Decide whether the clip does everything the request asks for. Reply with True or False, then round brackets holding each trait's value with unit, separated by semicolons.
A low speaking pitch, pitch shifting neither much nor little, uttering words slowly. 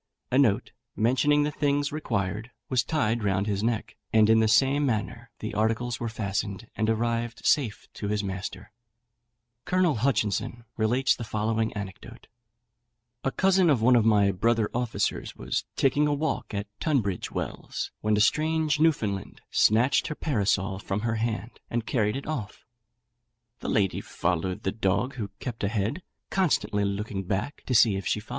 True (115 Hz; 4.3 semitones; 130 wpm)